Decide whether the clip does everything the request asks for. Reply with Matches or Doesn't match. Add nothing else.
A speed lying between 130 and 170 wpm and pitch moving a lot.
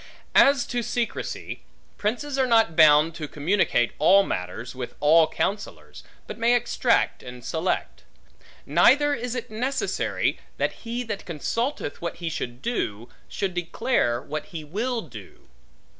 Matches